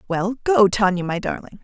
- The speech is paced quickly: No, average, 185 wpm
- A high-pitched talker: Yes, high, 205 Hz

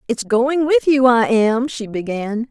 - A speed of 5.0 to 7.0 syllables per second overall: No, 4.1 syllables/s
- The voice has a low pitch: No, high, 240 Hz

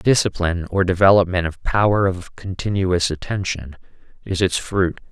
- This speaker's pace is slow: Yes, slow, 130 wpm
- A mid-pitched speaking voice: No, very low, 90 Hz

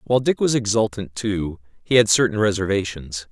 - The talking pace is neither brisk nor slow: Yes, average, 165 wpm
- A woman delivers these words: No, male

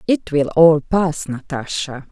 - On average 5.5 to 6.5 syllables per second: No, 3.6 syllables/s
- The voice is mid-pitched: Yes, medium, 155 Hz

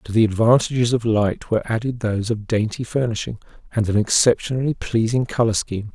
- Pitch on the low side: Yes, low, 115 Hz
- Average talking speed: Yes, average, 170 wpm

